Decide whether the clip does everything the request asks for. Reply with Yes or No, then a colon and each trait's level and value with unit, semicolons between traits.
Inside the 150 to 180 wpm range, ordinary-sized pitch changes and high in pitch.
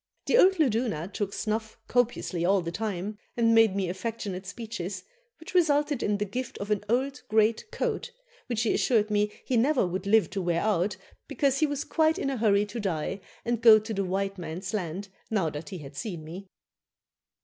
No: average, 195 wpm; average, 3.9 semitones; high, 210 Hz